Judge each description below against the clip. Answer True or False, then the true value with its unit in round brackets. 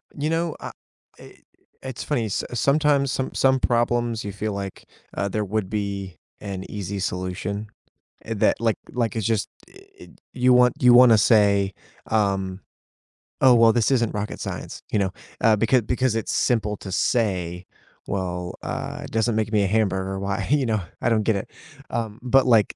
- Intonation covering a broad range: False (3.5 semitones)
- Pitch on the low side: True (110 Hz)